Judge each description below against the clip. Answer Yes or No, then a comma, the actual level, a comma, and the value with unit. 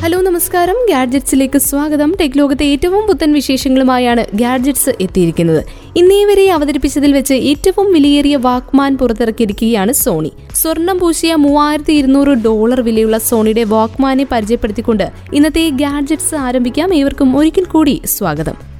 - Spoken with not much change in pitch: No, average, 4.7 semitones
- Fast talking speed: No, average, 110 wpm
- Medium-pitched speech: No, very high, 280 Hz